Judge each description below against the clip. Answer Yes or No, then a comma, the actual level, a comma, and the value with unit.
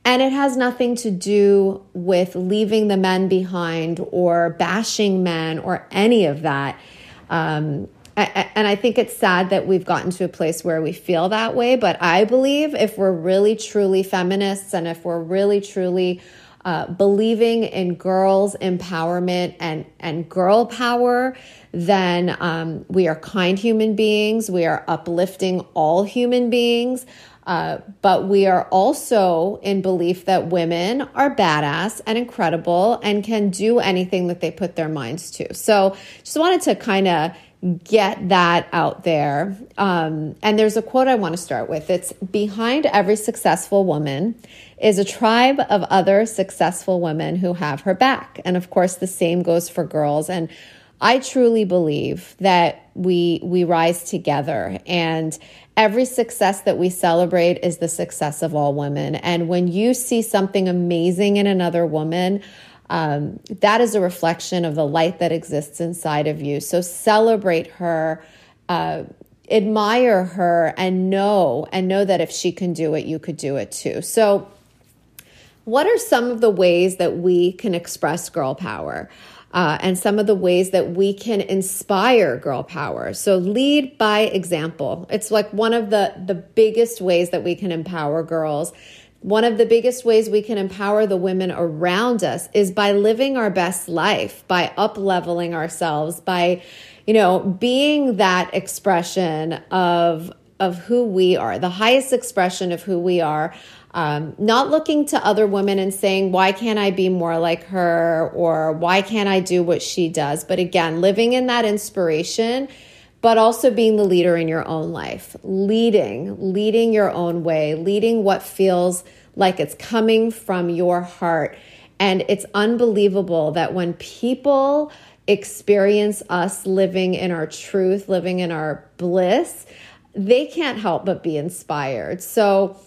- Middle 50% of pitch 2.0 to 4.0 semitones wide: Yes, average, 3.7 semitones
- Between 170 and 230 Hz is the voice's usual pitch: Yes, medium, 185 Hz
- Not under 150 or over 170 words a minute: Yes, average, 160 wpm